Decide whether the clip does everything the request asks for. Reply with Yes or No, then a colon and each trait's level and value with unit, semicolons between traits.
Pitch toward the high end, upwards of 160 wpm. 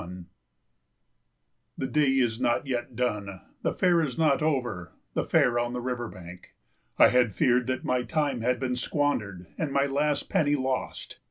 No: low, 125 Hz; average, 170 wpm